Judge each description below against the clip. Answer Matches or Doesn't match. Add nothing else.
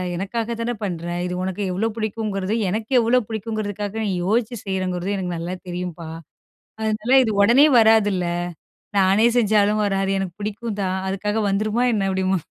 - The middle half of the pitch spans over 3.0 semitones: Doesn't match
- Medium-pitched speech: Doesn't match